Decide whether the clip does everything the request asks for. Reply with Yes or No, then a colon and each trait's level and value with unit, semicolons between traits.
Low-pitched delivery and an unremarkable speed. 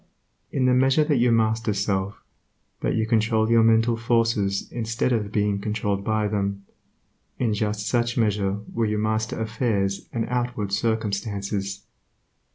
Yes: low, 110 Hz; average, 145 wpm